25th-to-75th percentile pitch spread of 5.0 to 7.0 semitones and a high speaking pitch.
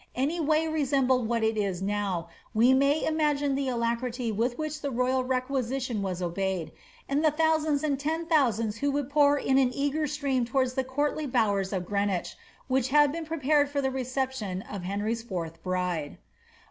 Yes: average, 5.3 semitones; very high, 260 Hz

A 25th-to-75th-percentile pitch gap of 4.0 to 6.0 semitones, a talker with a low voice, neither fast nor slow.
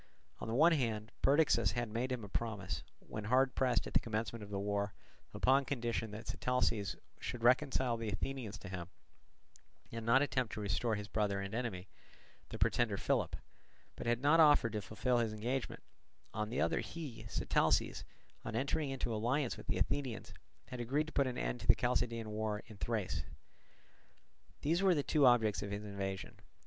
No: average, 3.6 semitones; low, 115 Hz; average, 180 wpm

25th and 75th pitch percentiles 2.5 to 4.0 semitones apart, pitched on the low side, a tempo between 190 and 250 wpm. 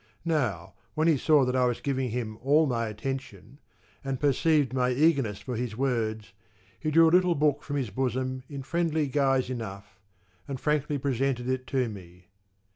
No: average, 3.5 semitones; low, 130 Hz; average, 175 wpm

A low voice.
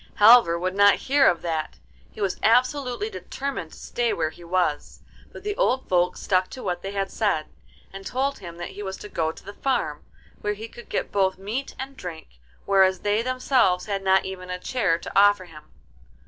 No: high, 195 Hz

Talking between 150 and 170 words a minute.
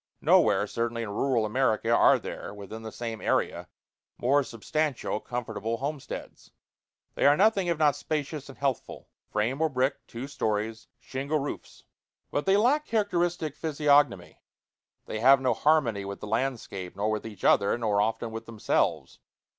Yes: average, 155 wpm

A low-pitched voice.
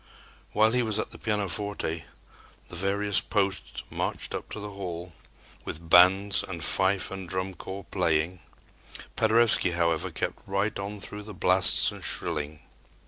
Yes: very low, 95 Hz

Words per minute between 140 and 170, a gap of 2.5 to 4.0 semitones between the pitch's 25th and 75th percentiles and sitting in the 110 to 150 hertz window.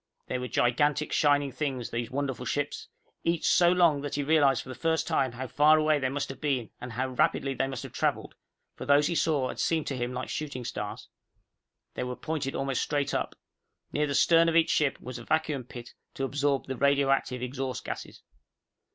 No: fast, 205 wpm; average, 2.8 semitones; medium, 140 Hz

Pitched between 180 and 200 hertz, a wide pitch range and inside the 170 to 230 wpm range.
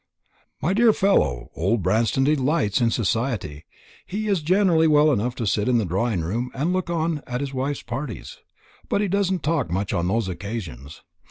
No: low, 125 Hz; wide, 8.0 semitones; average, 175 wpm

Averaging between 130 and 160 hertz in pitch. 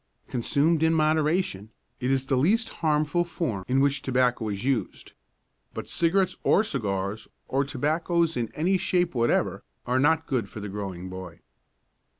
Yes: medium, 140 Hz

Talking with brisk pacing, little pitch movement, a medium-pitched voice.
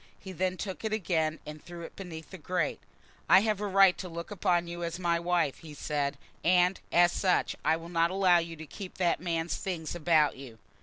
Yes: fast, 215 wpm; narrow, 2.1 semitones; medium, 175 Hz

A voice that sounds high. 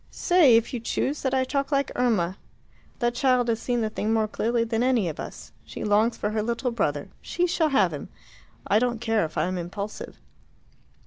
Yes: high, 235 Hz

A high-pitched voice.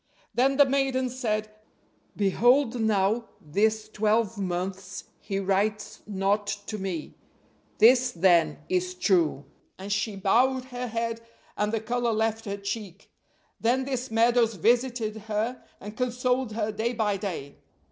Yes: high, 220 Hz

